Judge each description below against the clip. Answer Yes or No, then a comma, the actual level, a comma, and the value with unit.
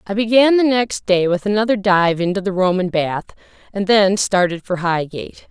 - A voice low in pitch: No, high, 195 Hz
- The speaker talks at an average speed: Yes, average, 185 wpm